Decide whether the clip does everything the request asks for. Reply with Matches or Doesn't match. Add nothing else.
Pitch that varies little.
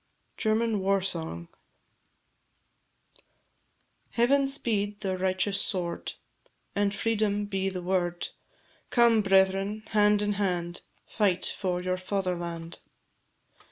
Matches